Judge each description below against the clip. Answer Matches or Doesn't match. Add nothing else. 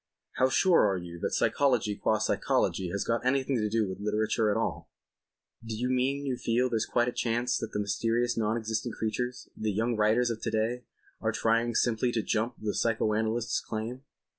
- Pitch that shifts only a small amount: Matches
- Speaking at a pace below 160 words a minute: Doesn't match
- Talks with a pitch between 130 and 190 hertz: Doesn't match